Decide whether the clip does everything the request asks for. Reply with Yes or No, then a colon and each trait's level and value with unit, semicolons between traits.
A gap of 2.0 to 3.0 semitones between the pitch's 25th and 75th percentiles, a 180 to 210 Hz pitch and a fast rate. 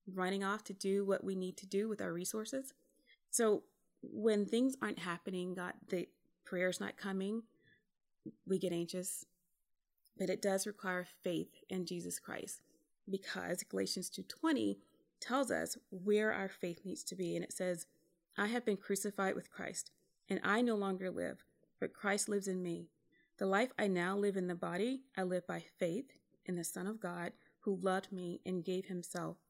No: narrow, 2.5 semitones; high, 190 Hz; average, 175 wpm